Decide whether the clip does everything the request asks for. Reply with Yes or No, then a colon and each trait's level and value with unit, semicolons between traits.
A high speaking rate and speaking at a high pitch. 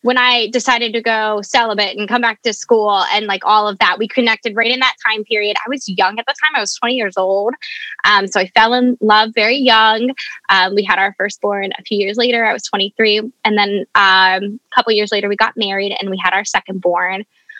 Yes: fast, 240 wpm; high, 215 Hz